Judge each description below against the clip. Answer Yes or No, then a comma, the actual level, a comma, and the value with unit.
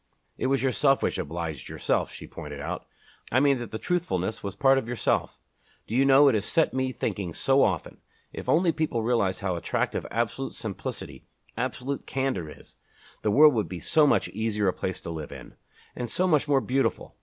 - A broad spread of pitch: Yes, wide, 6.2 semitones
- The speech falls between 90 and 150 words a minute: No, average, 195 wpm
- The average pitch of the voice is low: Yes, low, 120 Hz